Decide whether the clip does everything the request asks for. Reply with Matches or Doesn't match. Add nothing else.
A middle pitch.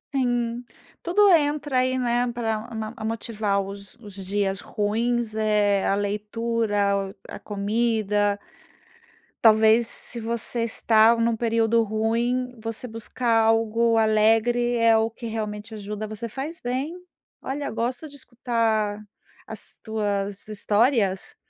Doesn't match